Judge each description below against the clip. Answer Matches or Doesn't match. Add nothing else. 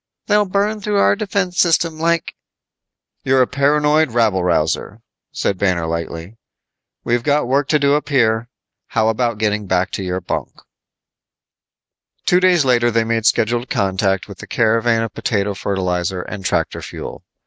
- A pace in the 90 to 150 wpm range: Doesn't match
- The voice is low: Matches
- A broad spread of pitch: Matches